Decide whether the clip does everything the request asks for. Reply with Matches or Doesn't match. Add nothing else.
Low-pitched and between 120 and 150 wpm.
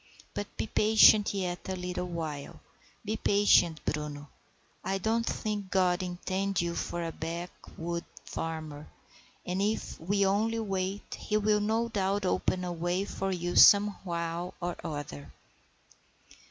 Doesn't match